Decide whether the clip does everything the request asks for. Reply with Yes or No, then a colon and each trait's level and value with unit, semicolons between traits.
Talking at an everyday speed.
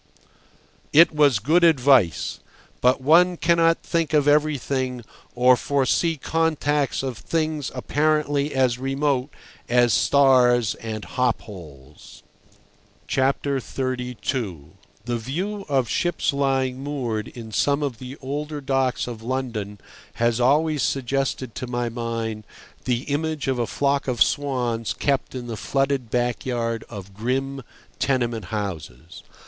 No: slow, 120 wpm